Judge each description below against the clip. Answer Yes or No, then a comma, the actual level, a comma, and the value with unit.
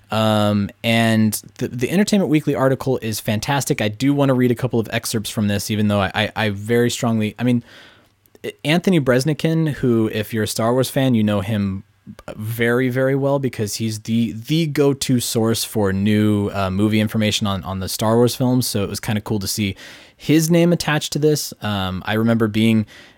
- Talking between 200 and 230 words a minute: Yes, fast, 205 wpm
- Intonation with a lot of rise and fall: No, average, 3.8 semitones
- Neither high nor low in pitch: No, low, 115 Hz